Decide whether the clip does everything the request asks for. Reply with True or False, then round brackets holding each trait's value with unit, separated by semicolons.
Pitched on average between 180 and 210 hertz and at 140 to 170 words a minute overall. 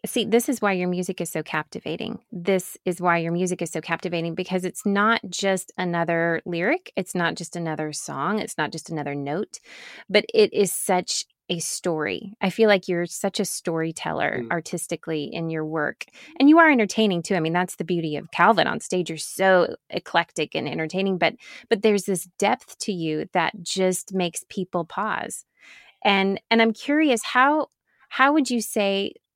False (185 Hz; 185 wpm)